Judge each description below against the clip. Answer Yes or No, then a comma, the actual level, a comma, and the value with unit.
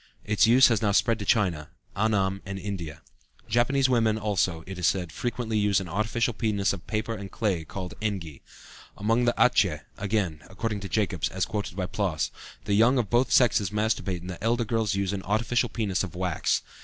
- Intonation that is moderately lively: Yes, average, 3.2 semitones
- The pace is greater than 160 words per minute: Yes, average, 190 wpm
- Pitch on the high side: No, low, 105 Hz